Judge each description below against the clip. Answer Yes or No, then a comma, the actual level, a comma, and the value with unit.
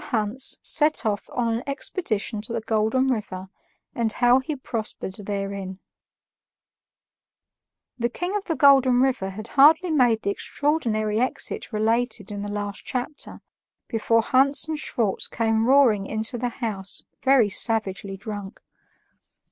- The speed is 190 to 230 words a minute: No, slow, 135 wpm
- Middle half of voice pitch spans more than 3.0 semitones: Yes, average, 4.0 semitones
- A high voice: Yes, high, 230 Hz